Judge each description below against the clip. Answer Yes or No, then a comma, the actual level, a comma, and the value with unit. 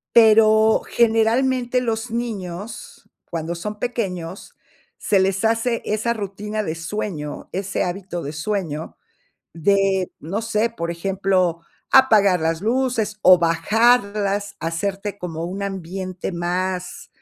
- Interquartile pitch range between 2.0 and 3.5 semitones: No, average, 4.0 semitones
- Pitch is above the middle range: Yes, high, 200 Hz